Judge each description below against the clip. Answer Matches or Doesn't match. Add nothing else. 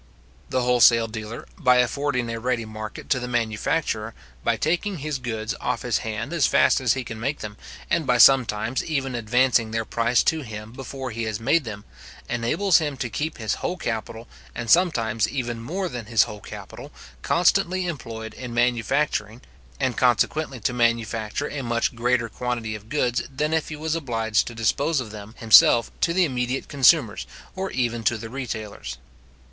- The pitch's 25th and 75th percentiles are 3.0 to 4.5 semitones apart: Matches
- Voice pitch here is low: Matches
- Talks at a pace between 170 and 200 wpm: Matches